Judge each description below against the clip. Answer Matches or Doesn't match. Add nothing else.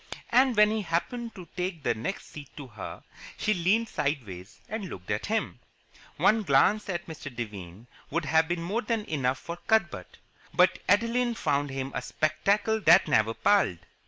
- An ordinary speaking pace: Matches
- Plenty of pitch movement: Matches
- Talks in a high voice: Doesn't match